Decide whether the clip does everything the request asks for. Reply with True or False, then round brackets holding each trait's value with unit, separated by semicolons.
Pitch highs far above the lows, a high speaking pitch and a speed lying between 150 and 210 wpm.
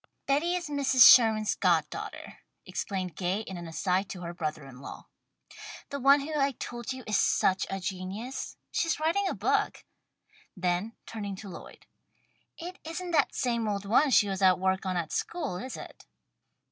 True (7.0 semitones; 215 Hz; 175 wpm)